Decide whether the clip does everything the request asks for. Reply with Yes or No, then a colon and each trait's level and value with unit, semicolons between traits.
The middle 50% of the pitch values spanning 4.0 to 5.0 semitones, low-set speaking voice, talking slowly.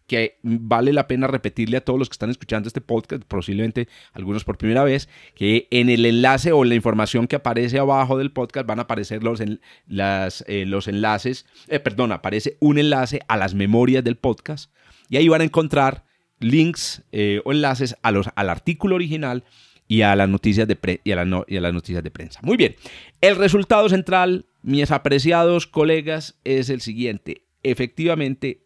No: average, 4.6 semitones; low, 125 Hz; fast, 190 wpm